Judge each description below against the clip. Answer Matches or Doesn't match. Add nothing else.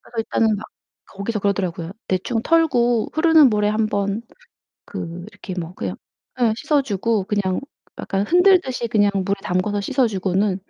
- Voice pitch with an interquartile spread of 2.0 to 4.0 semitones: Matches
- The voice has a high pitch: Matches